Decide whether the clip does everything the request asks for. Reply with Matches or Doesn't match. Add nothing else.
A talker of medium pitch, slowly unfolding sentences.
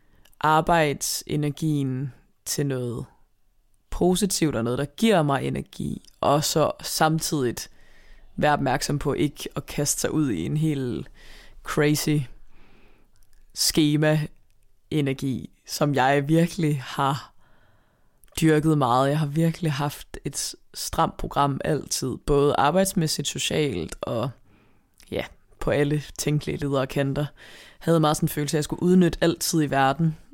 Matches